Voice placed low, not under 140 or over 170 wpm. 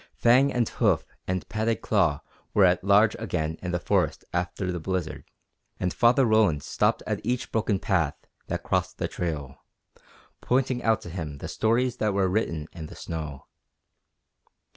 Yes: very low, 95 Hz; average, 165 wpm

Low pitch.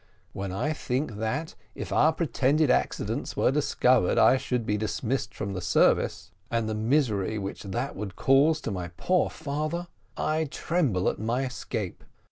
Yes: low, 125 Hz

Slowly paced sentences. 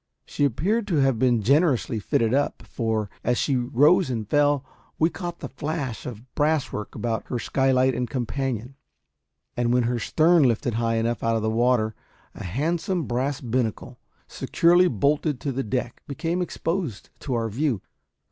No: average, 165 wpm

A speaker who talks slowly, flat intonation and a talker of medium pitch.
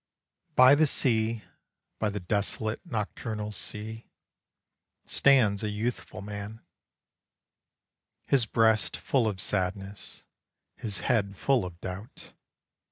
No: slow, 100 wpm; narrow, 2.2 semitones; low, 110 Hz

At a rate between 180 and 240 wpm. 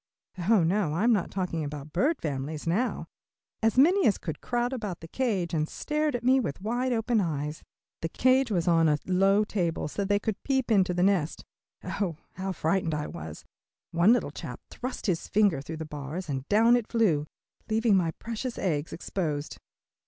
Yes: average, 185 wpm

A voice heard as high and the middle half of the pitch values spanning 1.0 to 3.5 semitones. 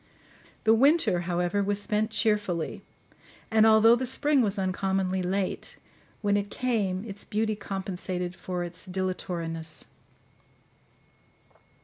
Yes: high, 195 Hz; average, 3.1 semitones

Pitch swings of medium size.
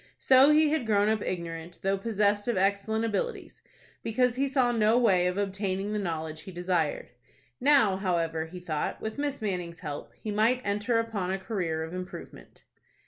Yes: average, 4.1 semitones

